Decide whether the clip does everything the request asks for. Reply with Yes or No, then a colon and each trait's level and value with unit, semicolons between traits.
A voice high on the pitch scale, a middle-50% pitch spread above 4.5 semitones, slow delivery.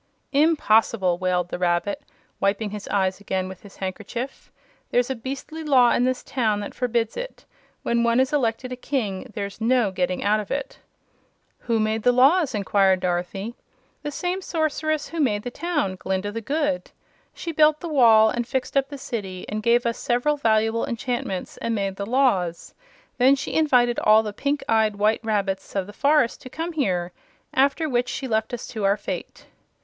No: high, 230 Hz; average, 5.1 semitones; average, 185 wpm